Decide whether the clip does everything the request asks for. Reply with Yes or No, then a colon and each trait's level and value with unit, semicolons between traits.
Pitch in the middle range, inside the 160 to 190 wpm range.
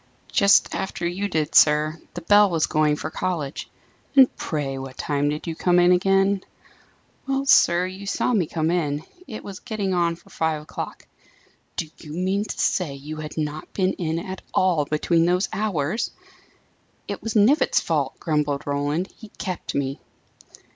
Yes: medium, 170 Hz; average, 170 wpm